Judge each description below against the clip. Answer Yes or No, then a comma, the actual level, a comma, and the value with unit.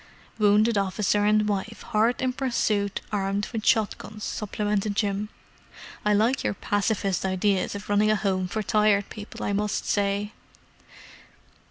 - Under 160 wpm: Yes, average, 145 wpm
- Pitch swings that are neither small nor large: No, narrow, 1.1 semitones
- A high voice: Yes, high, 205 Hz